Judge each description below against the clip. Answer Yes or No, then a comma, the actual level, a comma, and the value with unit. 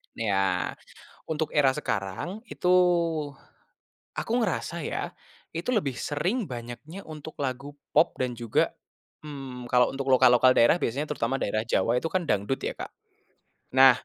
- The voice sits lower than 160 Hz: Yes, low, 135 Hz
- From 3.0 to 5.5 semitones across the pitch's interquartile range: Yes, average, 4.5 semitones